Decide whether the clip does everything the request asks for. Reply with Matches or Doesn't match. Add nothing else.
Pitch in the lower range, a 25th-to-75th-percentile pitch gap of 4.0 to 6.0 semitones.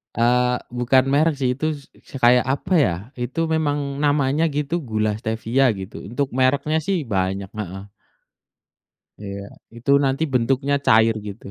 Matches